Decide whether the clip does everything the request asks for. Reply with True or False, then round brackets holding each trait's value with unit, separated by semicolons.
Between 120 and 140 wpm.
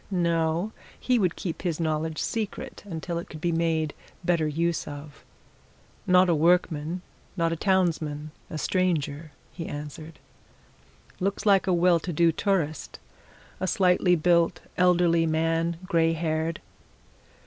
True (135 wpm)